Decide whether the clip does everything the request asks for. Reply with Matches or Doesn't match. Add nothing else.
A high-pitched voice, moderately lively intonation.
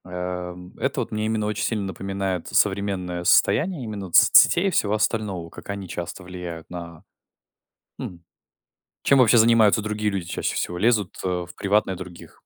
Doesn't match